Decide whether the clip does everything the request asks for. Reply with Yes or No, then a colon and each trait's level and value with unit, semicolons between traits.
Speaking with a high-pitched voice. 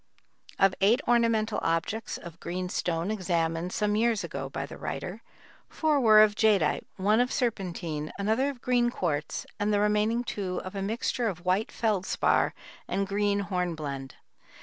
Yes: high, 205 Hz